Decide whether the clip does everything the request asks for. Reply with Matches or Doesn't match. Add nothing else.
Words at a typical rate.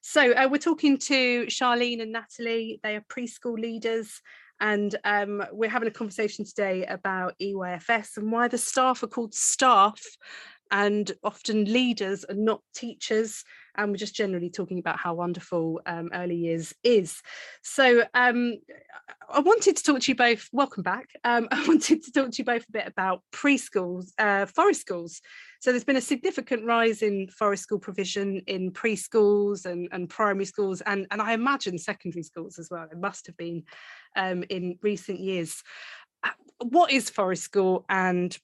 Matches